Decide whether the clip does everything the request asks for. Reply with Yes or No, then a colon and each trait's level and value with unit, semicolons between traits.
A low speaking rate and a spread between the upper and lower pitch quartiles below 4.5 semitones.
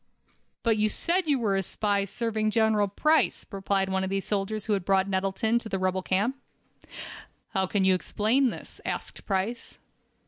No: average, 175 wpm; average, 2.7 semitones